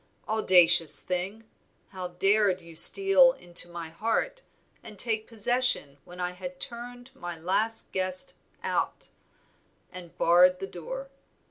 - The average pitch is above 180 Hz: Yes, high, 190 Hz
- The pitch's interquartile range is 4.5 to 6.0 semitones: Yes, average, 4.9 semitones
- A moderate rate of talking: No, slow, 125 wpm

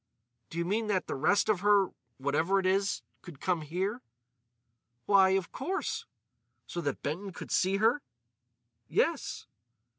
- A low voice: No, high, 190 Hz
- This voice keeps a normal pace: No, slow, 130 wpm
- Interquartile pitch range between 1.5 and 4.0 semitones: Yes, average, 3.2 semitones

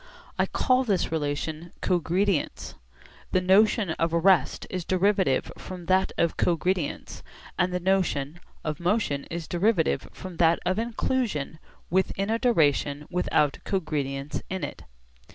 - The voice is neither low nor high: Yes, medium, 180 Hz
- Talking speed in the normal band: No, slow, 130 wpm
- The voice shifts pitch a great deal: No, average, 3.5 semitones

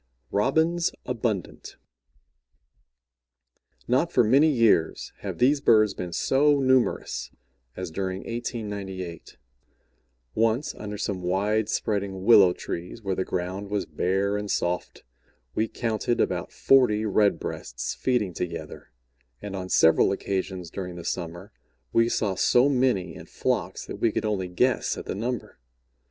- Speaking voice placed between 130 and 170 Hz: No, low, 105 Hz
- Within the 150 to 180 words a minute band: No, slow, 135 wpm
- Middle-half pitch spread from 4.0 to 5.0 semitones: Yes, average, 4.4 semitones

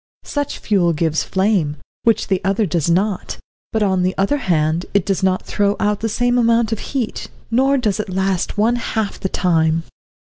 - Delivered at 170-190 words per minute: Yes, average, 185 wpm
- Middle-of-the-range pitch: No, high, 200 Hz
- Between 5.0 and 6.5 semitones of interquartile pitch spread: No, average, 3.7 semitones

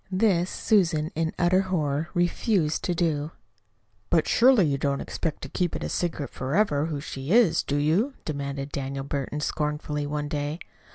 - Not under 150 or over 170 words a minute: Yes, average, 160 wpm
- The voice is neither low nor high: Yes, medium, 155 Hz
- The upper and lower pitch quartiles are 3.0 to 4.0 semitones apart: Yes, average, 3.4 semitones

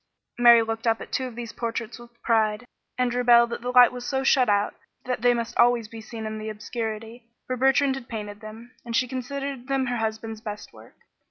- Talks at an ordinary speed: No, fast, 220 wpm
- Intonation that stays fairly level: Yes, narrow, 2.0 semitones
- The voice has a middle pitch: No, high, 235 Hz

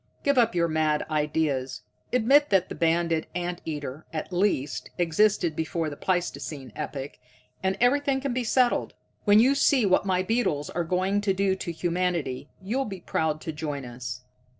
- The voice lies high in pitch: No, medium, 175 Hz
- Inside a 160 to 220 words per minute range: Yes, average, 170 wpm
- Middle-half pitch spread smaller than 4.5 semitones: No, average, 5.2 semitones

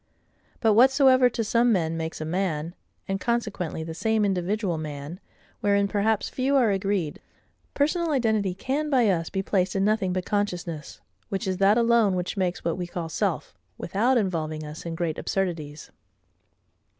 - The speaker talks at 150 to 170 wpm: Yes, average, 160 wpm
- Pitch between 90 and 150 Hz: No, high, 195 Hz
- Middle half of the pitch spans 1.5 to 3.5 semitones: No, average, 4.7 semitones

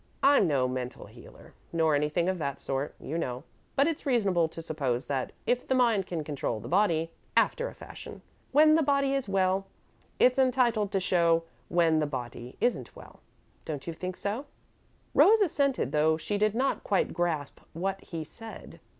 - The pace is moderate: Yes, average, 180 wpm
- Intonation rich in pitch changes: Yes, wide, 8.1 semitones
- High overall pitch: No, medium, 180 Hz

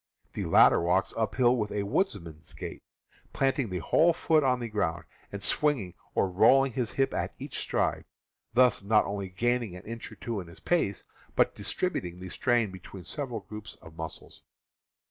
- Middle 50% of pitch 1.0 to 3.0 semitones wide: No, wide, 5.4 semitones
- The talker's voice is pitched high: No, low, 105 Hz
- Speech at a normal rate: Yes, average, 180 wpm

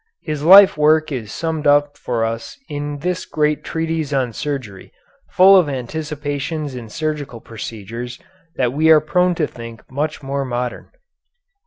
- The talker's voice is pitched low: No, medium, 145 Hz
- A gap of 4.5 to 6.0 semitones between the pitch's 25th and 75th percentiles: No, average, 4.1 semitones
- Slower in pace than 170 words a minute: Yes, average, 150 wpm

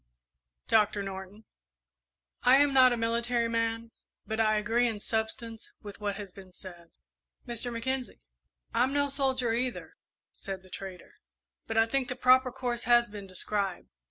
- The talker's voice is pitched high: Yes, high, 230 Hz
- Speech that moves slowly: No, average, 155 wpm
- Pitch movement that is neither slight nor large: Yes, average, 3.2 semitones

